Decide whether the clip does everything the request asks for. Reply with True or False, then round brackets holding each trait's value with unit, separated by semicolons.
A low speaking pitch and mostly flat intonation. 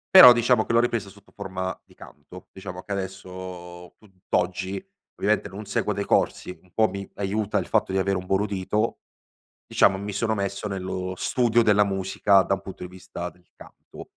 True (95 Hz; 2.0 semitones)